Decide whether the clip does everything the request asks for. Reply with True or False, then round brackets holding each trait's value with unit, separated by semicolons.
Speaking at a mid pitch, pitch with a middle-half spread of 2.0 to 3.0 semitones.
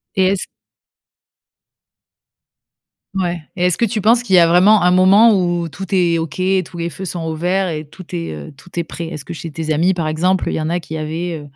True (175 Hz; 2.6 semitones)